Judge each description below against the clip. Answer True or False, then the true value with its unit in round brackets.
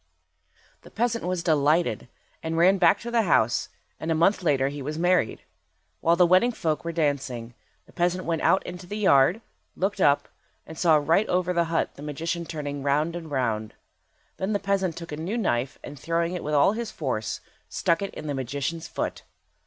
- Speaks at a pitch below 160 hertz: False (165 Hz)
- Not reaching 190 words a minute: False (195 wpm)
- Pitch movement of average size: True (4.0 semitones)